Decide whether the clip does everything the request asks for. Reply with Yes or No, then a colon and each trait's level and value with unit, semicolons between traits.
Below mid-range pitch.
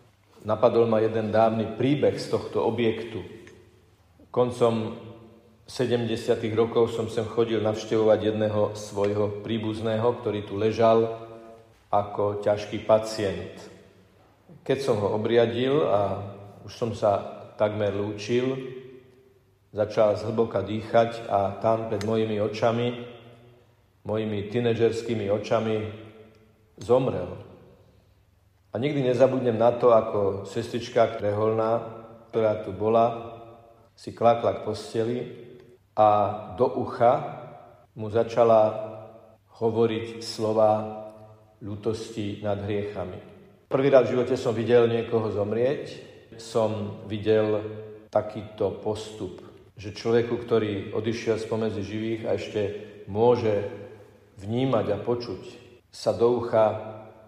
Yes: low, 110 Hz